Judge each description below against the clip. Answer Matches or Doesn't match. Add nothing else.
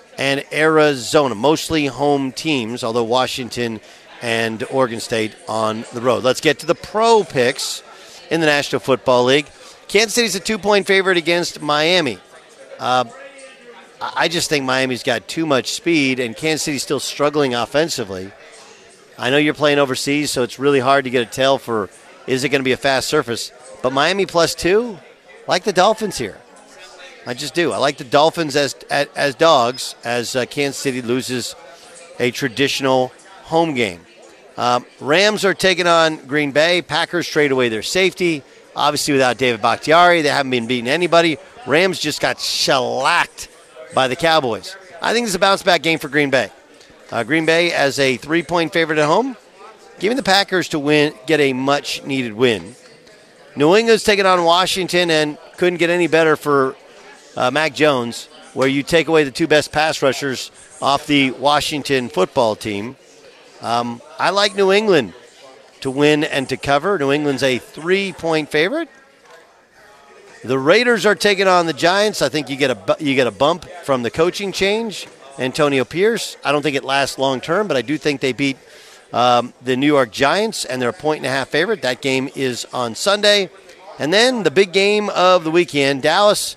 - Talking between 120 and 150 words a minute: Doesn't match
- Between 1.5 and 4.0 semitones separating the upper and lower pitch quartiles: Doesn't match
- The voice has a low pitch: Doesn't match